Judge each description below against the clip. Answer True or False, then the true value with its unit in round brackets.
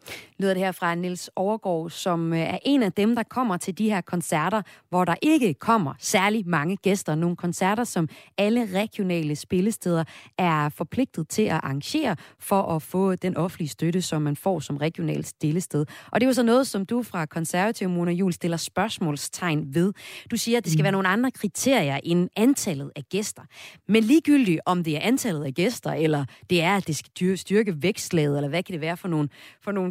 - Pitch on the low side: False (180 Hz)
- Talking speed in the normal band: True (200 wpm)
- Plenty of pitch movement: False (4.5 semitones)